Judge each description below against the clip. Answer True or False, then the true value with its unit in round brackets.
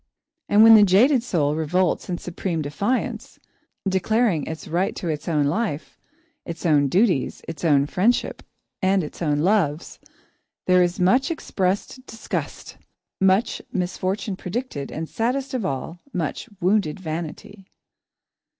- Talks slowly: True (130 wpm)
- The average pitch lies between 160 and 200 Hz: True (185 Hz)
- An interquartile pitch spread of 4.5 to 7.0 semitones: True (4.8 semitones)